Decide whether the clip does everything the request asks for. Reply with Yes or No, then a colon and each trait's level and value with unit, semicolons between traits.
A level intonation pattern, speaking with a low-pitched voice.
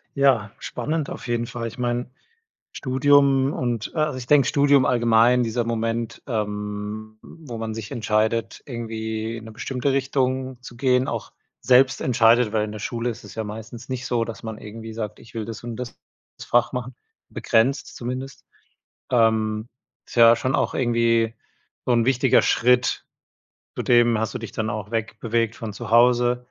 Yes: narrow, 2.1 semitones; low, 115 Hz